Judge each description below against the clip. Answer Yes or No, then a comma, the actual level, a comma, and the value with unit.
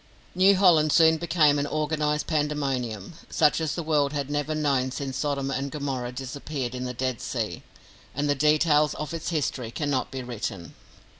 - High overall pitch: No, medium, 145 Hz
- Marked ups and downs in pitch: No, average, 2.7 semitones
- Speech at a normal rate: Yes, average, 170 wpm